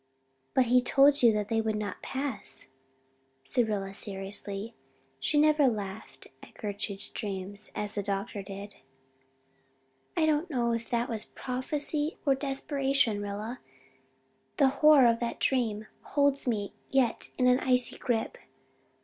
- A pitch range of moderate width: Yes, average, 4.7 semitones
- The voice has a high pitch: Yes, high, 235 Hz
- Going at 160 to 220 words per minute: No, average, 140 wpm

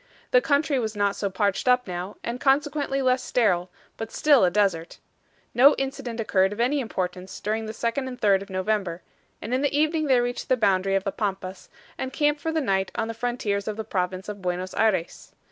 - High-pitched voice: Yes, high, 220 Hz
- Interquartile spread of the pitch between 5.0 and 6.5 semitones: Yes, average, 5.3 semitones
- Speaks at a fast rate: Yes, fast, 210 wpm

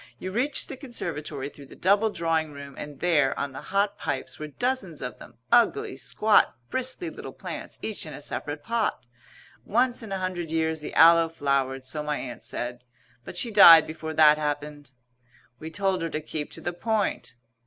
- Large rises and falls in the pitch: Yes, wide, 5.7 semitones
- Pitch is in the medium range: Yes, medium, 160 Hz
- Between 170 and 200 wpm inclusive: Yes, average, 190 wpm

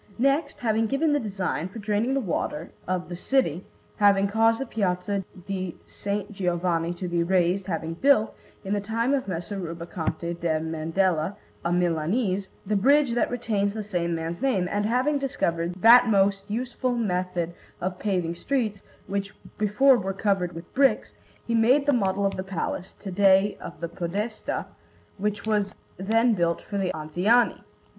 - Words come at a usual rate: Yes, average, 165 wpm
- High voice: Yes, high, 195 Hz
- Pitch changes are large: No, average, 4.2 semitones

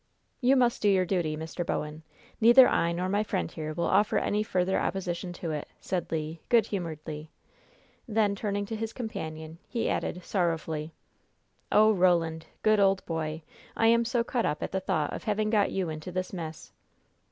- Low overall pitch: No, medium, 185 Hz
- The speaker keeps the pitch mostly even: No, average, 4.8 semitones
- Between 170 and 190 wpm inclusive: Yes, average, 180 wpm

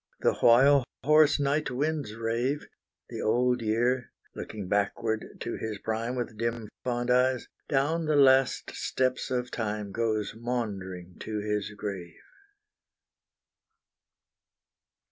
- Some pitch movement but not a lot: Yes, average, 3.3 semitones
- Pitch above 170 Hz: No, low, 120 Hz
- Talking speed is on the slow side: Yes, slow, 115 wpm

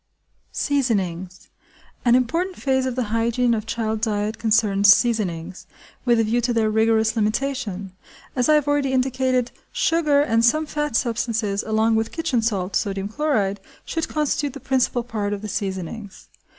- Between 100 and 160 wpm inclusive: Yes, average, 150 wpm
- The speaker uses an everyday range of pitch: Yes, average, 4.0 semitones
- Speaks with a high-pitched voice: Yes, high, 230 Hz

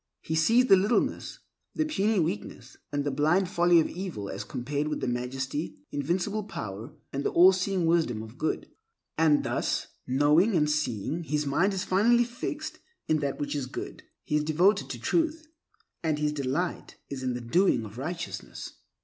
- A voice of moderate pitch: Yes, medium, 155 Hz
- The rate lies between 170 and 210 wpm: Yes, average, 175 wpm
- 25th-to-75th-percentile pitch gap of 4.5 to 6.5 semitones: Yes, average, 5.3 semitones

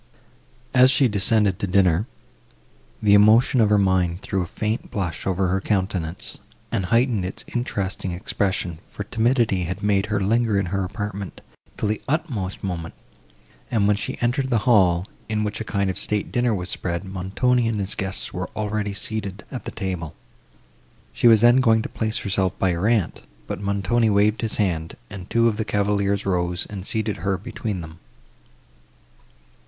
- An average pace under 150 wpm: No, average, 175 wpm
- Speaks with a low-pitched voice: Yes, low, 100 Hz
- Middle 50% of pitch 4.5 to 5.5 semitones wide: No, average, 2.9 semitones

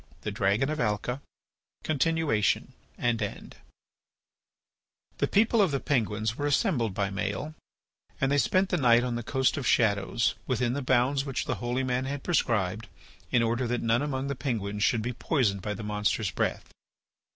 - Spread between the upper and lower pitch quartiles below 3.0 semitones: No, average, 4.4 semitones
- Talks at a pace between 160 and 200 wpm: Yes, average, 170 wpm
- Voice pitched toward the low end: Yes, low, 120 Hz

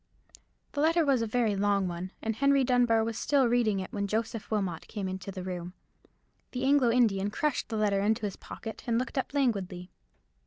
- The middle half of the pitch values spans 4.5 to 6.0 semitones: No, average, 4.1 semitones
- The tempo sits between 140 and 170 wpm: No, average, 195 wpm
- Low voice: No, high, 220 Hz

